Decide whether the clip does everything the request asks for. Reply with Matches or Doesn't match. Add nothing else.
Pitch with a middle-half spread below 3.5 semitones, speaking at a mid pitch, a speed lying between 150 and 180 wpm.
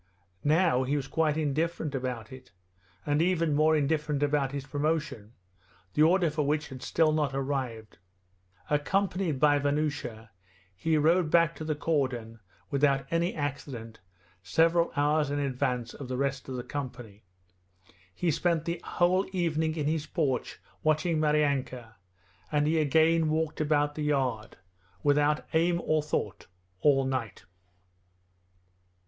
Doesn't match